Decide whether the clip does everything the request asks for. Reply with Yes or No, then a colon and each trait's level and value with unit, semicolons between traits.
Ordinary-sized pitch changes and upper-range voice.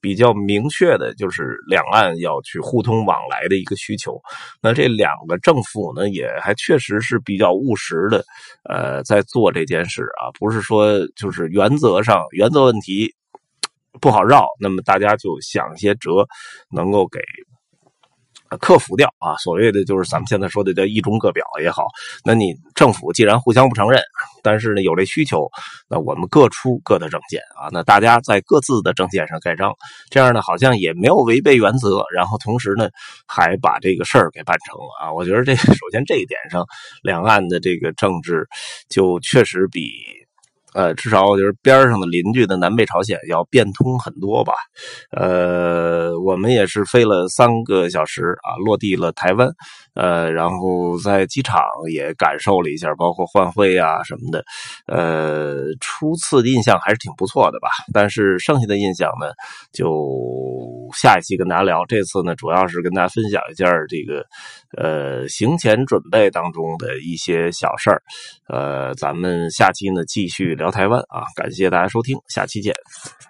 No: average, 4.6 semitones; low, 100 Hz